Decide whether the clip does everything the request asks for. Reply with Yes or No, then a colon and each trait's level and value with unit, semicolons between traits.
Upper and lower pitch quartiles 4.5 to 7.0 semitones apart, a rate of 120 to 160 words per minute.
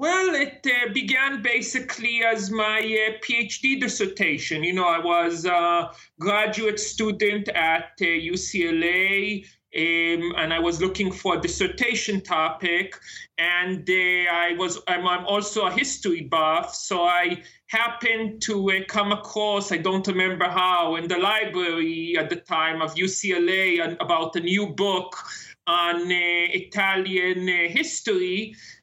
No: average, 3.9 semitones; slow, 135 wpm